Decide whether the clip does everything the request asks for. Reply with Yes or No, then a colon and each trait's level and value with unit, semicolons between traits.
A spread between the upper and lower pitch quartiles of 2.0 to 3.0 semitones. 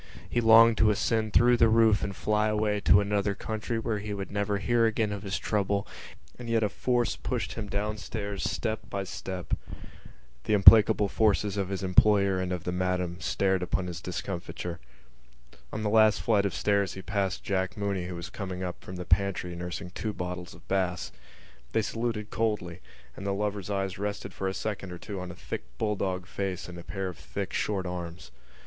Yes: narrow, 2.6 semitones